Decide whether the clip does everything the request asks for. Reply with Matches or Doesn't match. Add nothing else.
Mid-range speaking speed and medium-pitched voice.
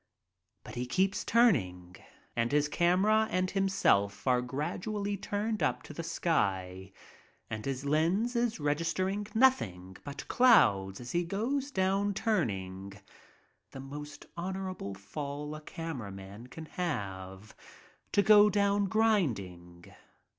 Doesn't match